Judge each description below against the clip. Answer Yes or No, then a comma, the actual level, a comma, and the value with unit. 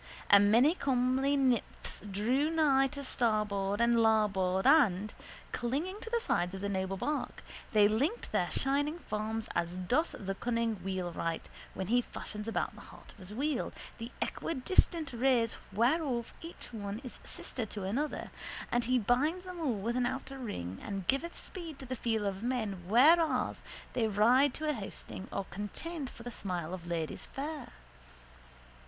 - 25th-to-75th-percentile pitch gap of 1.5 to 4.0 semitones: No, wide, 5.5 semitones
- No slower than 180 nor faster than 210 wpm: No, average, 165 wpm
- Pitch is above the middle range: Yes, high, 235 Hz